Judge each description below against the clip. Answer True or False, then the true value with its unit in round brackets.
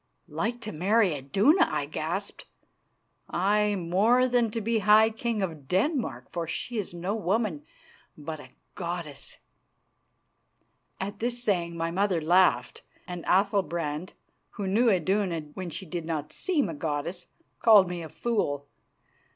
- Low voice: False (185 Hz)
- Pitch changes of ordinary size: True (4.6 semitones)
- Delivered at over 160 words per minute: False (140 wpm)